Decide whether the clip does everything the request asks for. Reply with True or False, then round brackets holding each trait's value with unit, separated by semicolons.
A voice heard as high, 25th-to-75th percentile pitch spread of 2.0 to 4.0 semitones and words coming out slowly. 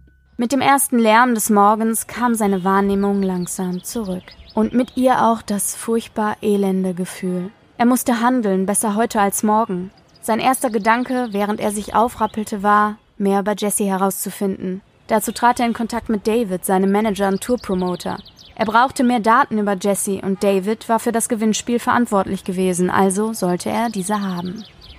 False (210 Hz; 2.9 semitones; 165 wpm)